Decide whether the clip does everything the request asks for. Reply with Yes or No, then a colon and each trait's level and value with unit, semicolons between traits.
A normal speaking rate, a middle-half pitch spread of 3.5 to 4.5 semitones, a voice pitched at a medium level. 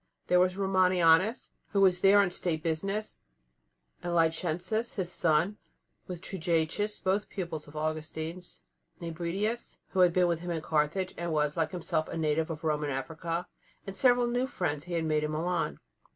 No: average, 165 wpm; average, 3.1 semitones; medium, 170 Hz